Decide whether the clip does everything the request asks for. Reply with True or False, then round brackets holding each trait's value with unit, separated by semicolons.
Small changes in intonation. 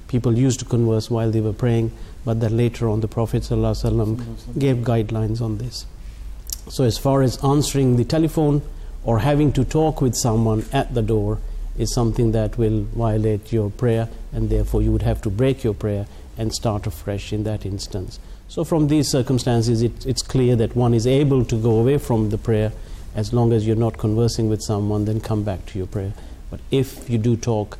True (2.3 semitones)